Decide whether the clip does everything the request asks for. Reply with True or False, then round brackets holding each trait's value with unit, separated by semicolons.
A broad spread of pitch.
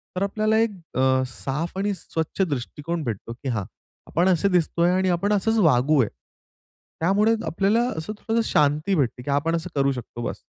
True (6.1 semitones)